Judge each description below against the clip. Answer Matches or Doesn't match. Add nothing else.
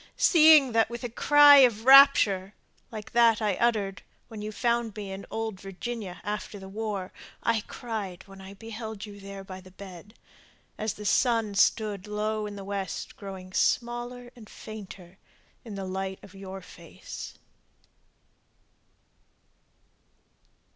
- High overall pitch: Matches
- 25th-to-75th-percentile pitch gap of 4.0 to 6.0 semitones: Doesn't match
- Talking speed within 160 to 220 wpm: Doesn't match